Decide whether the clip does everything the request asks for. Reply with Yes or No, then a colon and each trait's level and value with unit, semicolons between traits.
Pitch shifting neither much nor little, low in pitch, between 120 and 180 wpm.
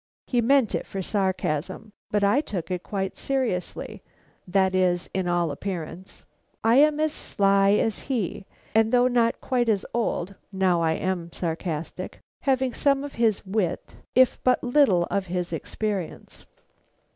No: average, 5.0 semitones; high, 200 Hz; average, 150 wpm